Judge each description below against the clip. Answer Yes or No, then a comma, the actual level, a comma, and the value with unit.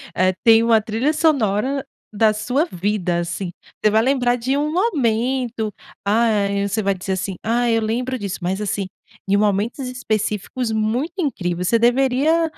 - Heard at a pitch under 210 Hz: No, high, 225 Hz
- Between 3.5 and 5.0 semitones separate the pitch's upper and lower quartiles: Yes, average, 4.1 semitones